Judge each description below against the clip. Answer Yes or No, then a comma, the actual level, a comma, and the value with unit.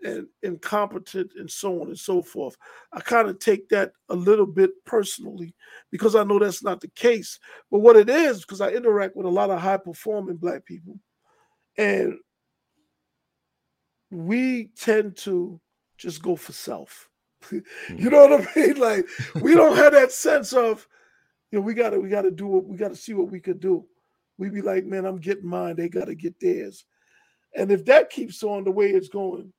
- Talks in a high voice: Yes, high, 205 Hz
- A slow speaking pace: No, average, 190 wpm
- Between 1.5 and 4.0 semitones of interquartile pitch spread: No, average, 5.2 semitones